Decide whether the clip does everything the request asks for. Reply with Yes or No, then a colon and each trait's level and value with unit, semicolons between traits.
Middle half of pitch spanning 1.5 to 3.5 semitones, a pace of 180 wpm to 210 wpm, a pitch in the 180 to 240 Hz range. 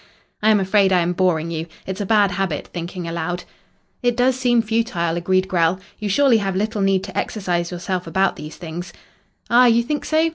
No: average, 4.1 semitones; average, 195 wpm; high, 190 Hz